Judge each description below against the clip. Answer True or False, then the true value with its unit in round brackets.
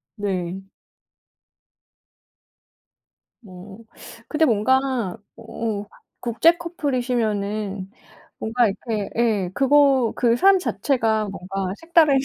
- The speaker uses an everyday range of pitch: True (4.9 semitones)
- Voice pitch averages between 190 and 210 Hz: False (225 Hz)